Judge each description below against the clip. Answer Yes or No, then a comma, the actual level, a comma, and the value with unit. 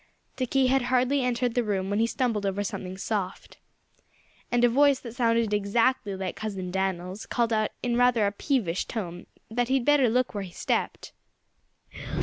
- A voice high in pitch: Yes, high, 230 Hz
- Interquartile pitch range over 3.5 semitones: Yes, average, 4.0 semitones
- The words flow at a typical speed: Yes, average, 175 wpm